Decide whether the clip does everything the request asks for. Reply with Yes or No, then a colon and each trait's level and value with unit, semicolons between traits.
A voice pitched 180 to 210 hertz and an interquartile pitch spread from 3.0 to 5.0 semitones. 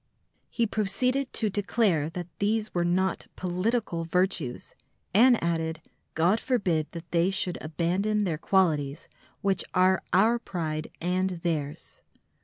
Yes: medium, 185 Hz; average, 3.8 semitones